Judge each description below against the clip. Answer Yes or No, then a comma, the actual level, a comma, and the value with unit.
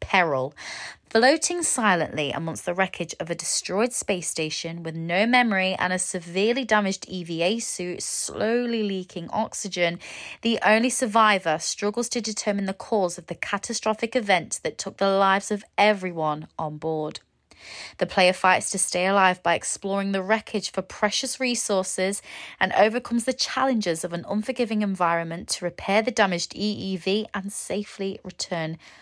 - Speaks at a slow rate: No, average, 150 wpm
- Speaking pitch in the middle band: No, high, 195 Hz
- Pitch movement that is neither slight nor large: Yes, average, 3.6 semitones